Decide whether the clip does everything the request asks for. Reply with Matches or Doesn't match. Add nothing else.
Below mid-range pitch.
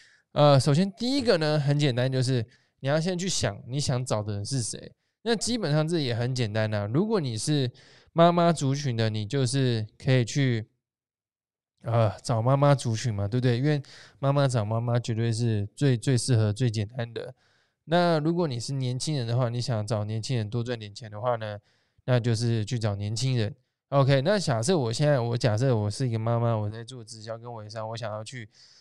Matches